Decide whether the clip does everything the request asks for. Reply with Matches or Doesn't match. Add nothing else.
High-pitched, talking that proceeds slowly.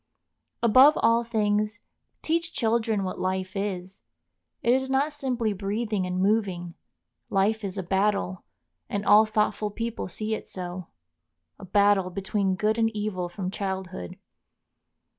Matches